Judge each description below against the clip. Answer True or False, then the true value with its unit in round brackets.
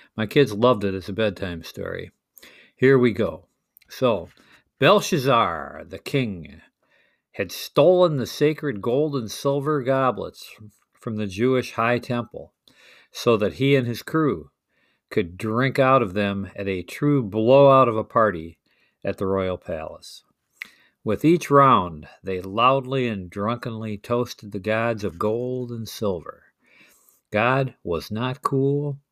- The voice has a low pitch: True (120 Hz)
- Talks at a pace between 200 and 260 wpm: False (140 wpm)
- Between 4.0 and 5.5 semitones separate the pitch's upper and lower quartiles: True (4.7 semitones)